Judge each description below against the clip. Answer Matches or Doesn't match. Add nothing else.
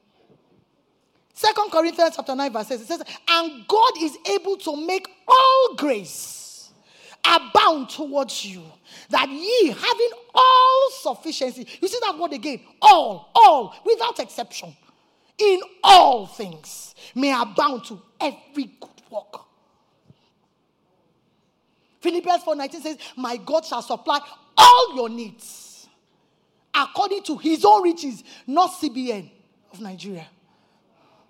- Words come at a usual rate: Doesn't match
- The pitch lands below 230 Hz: Doesn't match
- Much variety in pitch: Matches